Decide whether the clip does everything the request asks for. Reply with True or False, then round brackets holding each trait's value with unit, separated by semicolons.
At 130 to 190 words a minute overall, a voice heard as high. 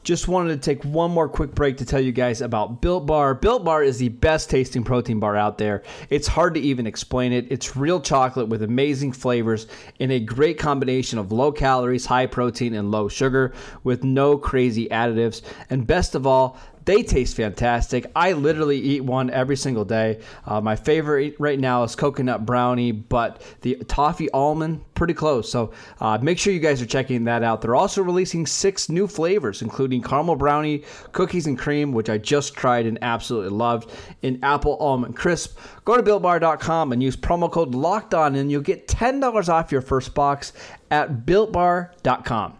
False (185 wpm; 135 Hz)